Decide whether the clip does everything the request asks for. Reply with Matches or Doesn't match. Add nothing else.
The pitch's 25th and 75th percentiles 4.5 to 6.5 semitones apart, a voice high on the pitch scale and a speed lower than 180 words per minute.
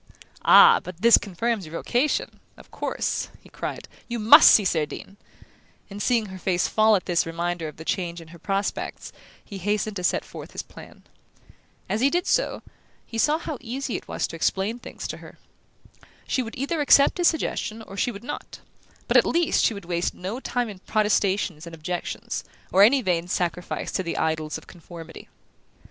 Doesn't match